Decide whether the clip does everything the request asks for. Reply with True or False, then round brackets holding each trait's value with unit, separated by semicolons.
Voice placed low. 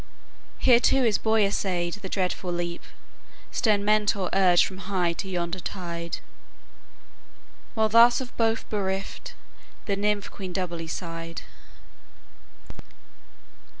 False (195 Hz)